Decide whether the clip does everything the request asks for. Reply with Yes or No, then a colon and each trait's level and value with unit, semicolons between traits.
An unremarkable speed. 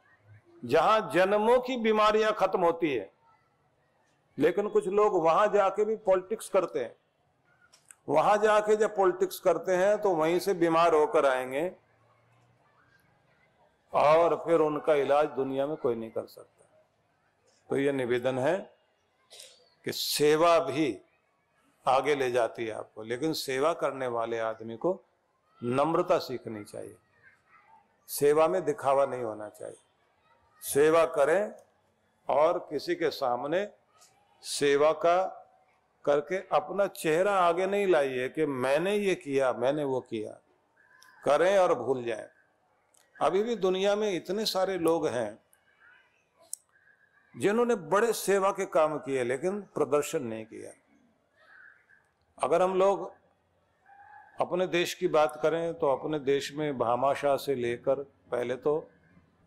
Yes: average, 125 wpm